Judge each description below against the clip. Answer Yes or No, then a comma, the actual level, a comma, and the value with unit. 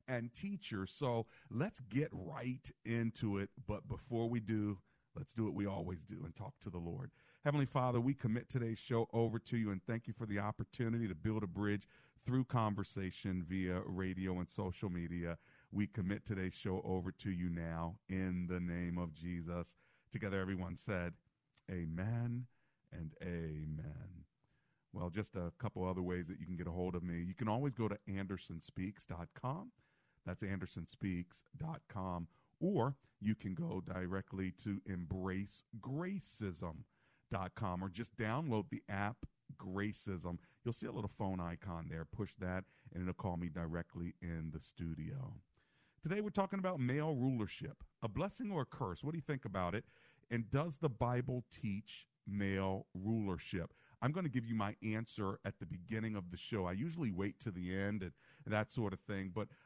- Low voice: Yes, low, 105 Hz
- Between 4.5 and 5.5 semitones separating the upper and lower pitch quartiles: Yes, average, 4.9 semitones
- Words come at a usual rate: Yes, average, 170 wpm